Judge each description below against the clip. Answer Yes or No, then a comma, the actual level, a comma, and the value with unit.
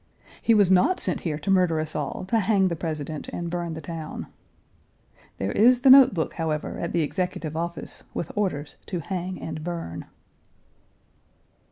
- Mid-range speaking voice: Yes, medium, 170 Hz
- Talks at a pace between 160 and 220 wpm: Yes, average, 170 wpm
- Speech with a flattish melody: No, average, 3.3 semitones